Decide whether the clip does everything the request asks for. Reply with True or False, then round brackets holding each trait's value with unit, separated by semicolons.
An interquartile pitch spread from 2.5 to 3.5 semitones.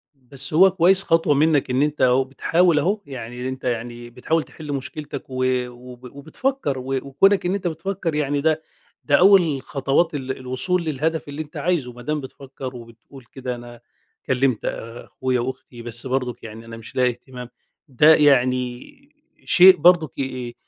False (4.1 semitones)